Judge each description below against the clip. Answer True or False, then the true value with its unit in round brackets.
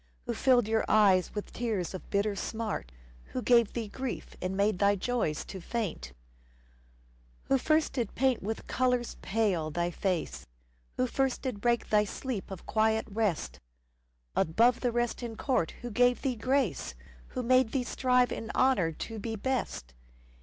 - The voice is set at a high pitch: True (225 Hz)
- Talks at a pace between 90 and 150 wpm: False (160 wpm)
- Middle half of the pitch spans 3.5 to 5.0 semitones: True (4.1 semitones)